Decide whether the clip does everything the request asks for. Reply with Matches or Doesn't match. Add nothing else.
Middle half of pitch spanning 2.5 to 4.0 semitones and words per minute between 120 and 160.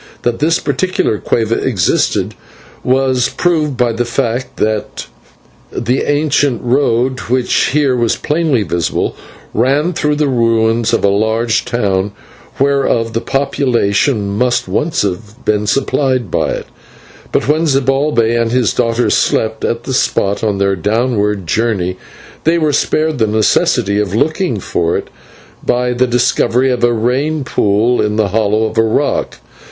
Matches